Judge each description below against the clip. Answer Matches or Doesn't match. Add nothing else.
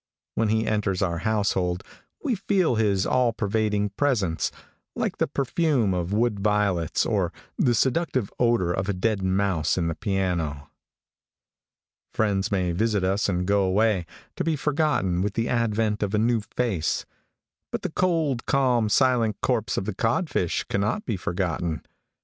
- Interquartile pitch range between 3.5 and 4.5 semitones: Matches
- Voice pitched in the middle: Doesn't match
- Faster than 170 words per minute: Doesn't match